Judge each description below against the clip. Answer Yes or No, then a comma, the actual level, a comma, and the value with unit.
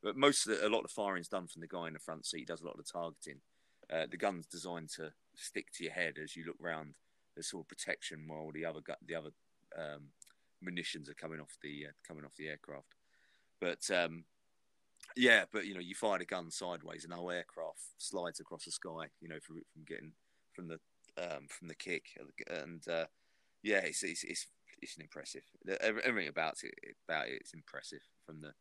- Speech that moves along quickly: Yes, fast, 225 wpm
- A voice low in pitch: Yes, very low, 80 Hz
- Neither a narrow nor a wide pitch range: No, narrow, 1.8 semitones